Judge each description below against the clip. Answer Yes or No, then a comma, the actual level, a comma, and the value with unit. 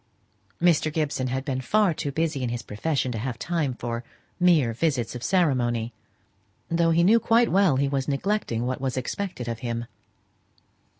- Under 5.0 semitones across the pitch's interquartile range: No, wide, 5.5 semitones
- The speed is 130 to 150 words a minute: No, average, 170 wpm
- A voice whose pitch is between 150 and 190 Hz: No, low, 135 Hz